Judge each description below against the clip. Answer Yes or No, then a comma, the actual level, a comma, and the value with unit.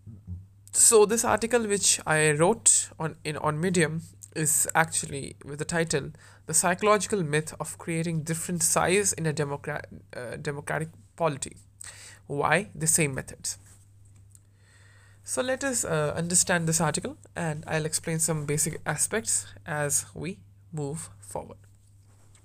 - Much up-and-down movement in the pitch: Yes, wide, 8.5 semitones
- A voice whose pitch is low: No, medium, 150 Hz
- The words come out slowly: Yes, slow, 130 wpm